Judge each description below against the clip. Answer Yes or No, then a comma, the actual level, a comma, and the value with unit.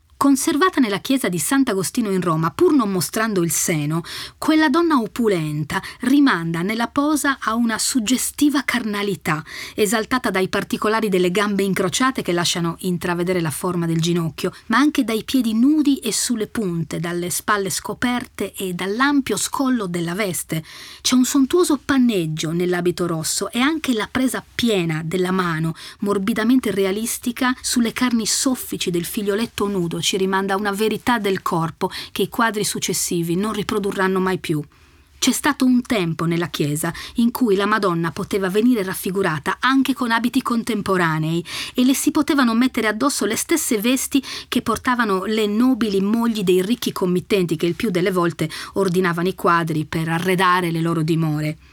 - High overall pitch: Yes, high, 205 Hz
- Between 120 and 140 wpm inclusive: No, average, 155 wpm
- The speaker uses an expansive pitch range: Yes, wide, 5.7 semitones